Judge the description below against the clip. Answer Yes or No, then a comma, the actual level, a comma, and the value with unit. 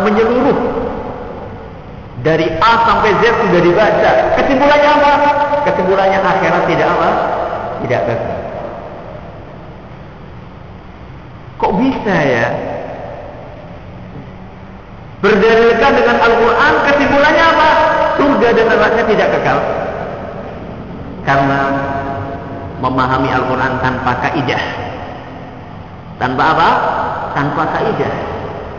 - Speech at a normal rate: No, slow, 75 wpm